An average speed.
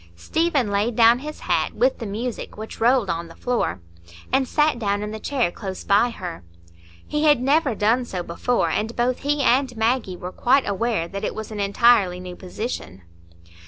Yes: average, 190 wpm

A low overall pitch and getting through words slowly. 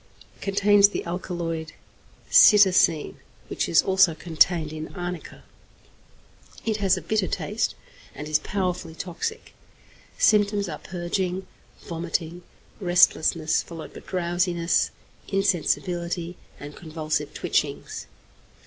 No: medium, 175 Hz; slow, 100 wpm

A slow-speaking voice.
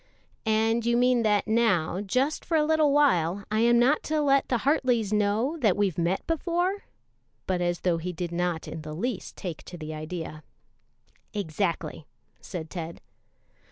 No: average, 165 wpm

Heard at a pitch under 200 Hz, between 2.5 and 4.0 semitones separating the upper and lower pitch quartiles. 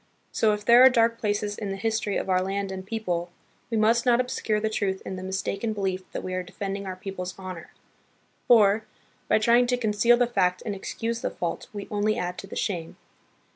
No: high, 205 Hz; average, 3.1 semitones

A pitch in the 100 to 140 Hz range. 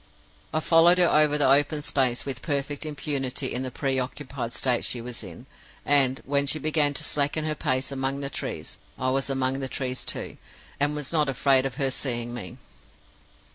Yes: low, 135 Hz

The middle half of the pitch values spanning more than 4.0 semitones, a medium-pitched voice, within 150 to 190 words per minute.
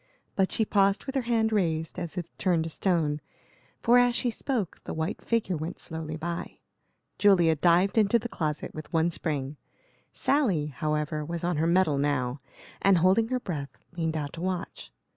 Yes: average, 4.4 semitones; medium, 170 Hz; average, 180 wpm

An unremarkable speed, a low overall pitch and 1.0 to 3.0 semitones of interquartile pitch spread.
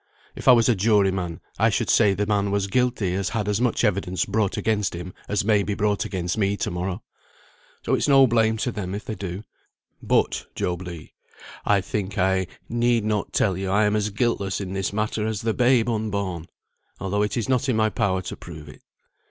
No: fast, 215 wpm; low, 100 Hz; average, 2.7 semitones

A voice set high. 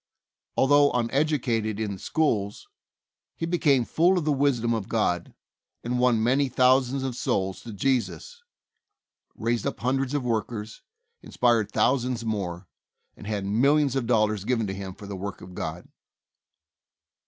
No: low, 120 Hz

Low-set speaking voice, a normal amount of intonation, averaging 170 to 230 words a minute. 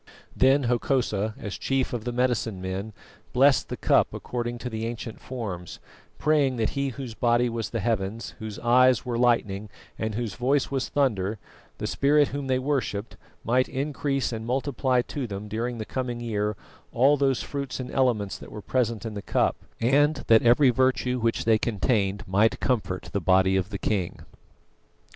Yes: low, 120 Hz; average, 3.4 semitones; average, 175 wpm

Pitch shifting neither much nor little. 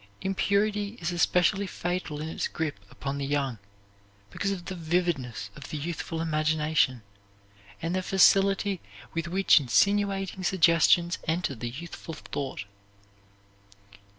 Yes: average, 4.2 semitones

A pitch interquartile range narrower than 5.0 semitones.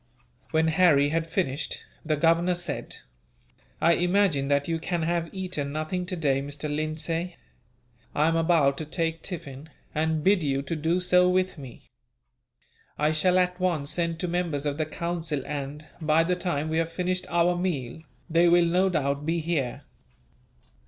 Yes: average, 2.8 semitones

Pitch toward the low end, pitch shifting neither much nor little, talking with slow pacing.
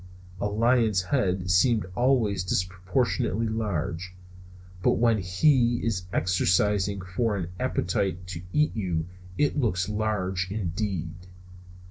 Yes: low, 100 Hz; average, 3.9 semitones; slow, 110 wpm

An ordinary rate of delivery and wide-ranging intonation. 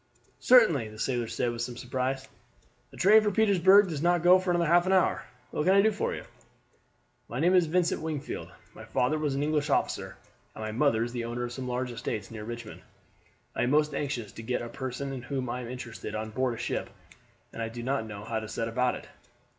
No: fast, 225 wpm; wide, 5.8 semitones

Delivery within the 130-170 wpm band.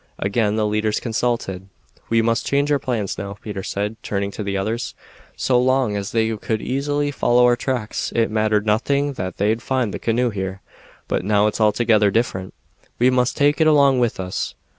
No: average, 185 wpm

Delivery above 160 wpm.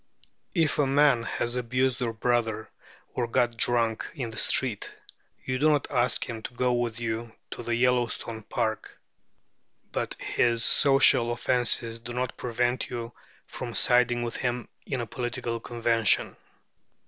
No: average, 150 wpm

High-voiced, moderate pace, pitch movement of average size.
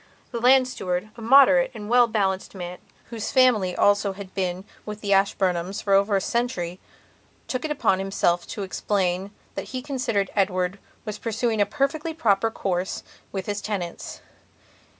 Yes: high, 205 Hz; average, 160 wpm; average, 3.9 semitones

